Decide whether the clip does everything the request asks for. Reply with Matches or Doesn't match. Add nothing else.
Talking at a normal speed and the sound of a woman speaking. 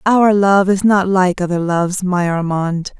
Matches